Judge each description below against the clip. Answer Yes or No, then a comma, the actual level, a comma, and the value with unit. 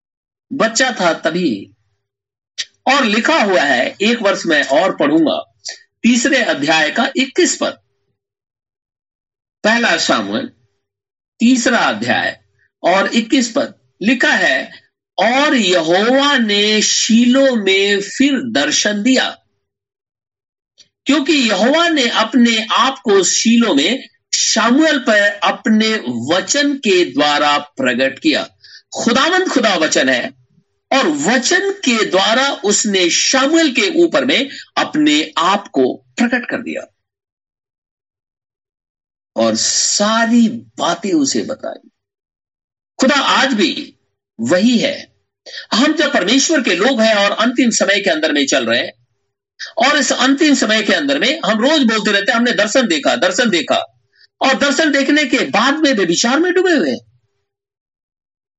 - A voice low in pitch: No, very high, 250 Hz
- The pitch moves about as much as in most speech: No, wide, 6.7 semitones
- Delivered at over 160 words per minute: No, average, 125 wpm